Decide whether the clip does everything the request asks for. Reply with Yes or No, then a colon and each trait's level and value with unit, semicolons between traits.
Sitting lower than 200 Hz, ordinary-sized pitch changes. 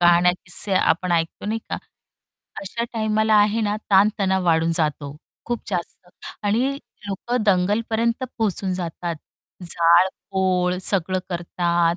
Yes: medium, 185 Hz; average, 3.6 semitones